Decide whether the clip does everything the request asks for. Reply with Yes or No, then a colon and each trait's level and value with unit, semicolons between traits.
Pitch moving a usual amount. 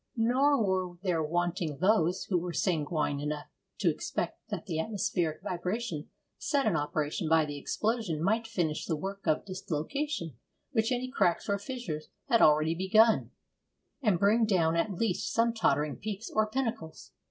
No: wide, 5.7 semitones